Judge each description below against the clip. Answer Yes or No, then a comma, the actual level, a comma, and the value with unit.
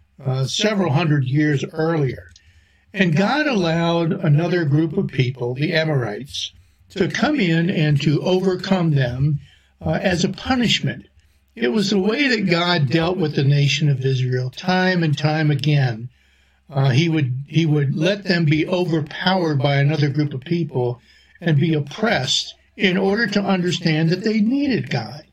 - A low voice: No, medium, 155 Hz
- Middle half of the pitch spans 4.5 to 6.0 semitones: Yes, average, 4.8 semitones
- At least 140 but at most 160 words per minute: Yes, average, 155 wpm